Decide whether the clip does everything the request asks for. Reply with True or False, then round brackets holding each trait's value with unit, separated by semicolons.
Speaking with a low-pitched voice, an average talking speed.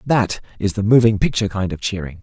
False (105 Hz; 215 wpm)